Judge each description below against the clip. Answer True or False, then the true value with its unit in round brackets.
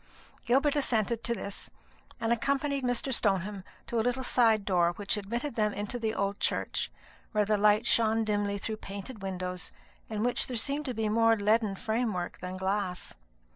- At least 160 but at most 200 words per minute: True (165 wpm)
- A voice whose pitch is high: True (215 Hz)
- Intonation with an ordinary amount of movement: True (3.1 semitones)